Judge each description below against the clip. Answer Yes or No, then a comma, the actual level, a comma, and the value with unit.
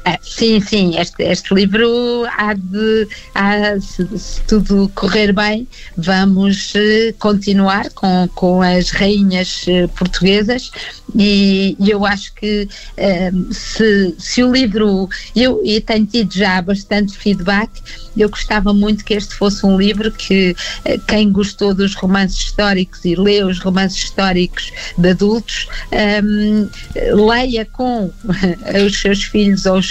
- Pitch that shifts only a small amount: Yes, narrow, 1.9 semitones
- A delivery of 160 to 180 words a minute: No, average, 140 wpm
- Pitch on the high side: Yes, high, 205 Hz